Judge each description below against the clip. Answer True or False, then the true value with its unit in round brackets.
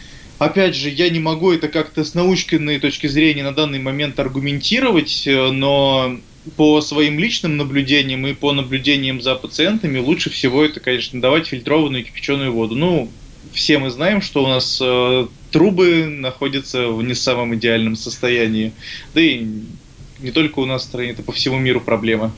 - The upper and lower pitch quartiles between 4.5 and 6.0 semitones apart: False (3.3 semitones)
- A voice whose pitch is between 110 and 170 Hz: True (140 Hz)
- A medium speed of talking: False (165 wpm)